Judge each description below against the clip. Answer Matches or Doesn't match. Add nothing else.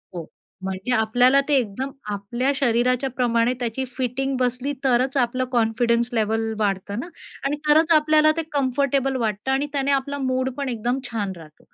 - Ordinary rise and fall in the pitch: Matches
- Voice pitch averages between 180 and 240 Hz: Doesn't match